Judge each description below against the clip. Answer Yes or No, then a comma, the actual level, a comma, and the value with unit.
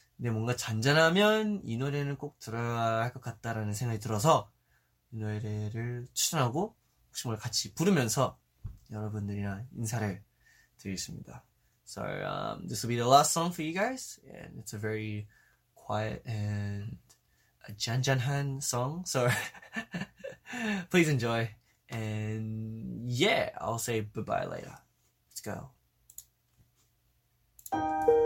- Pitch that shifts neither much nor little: Yes, average, 4.8 semitones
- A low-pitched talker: Yes, low, 120 Hz